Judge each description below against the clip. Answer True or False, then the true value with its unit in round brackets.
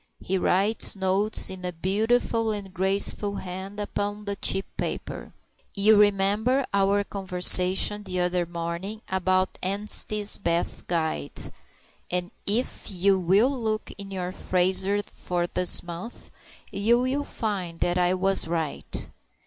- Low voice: False (195 Hz)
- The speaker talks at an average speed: False (130 wpm)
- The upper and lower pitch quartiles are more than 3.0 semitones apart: False (2.4 semitones)